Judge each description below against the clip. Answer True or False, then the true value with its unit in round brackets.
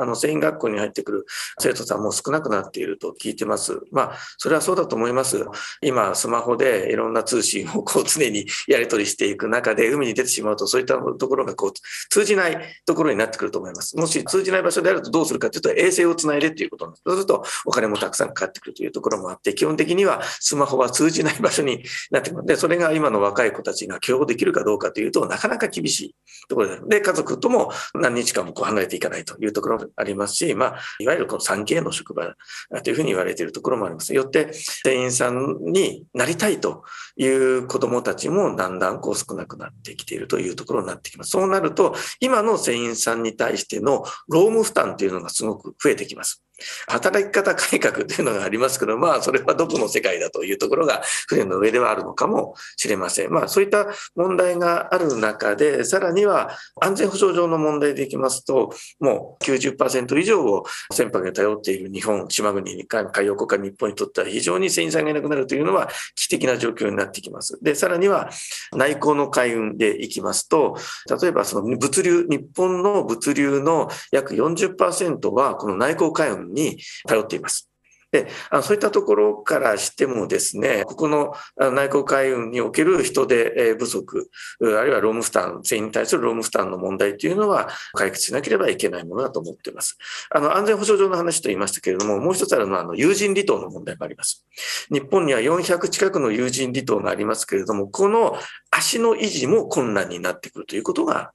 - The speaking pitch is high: True (200 Hz)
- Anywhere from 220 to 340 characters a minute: False (430 characters per minute)